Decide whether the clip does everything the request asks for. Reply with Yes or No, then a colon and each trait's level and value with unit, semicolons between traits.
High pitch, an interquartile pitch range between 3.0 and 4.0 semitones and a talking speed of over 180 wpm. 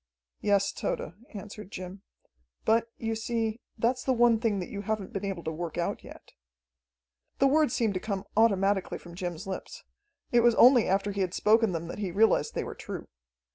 Yes: high, 205 Hz; average, 3.3 semitones; average, 190 wpm